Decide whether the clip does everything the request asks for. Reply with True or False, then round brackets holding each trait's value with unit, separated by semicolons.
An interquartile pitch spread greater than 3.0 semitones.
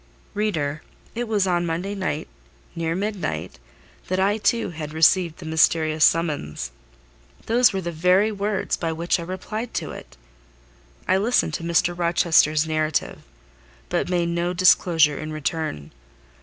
True (3.4 semitones)